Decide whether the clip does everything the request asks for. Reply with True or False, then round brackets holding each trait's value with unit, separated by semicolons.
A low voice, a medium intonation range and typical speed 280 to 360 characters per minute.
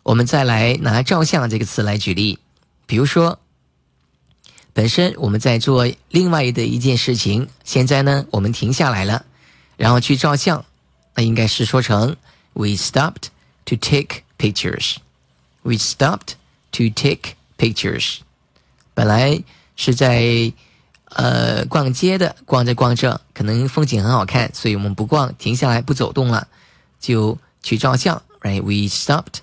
True (120 Hz; 4.4 semitones; 295 characters per minute)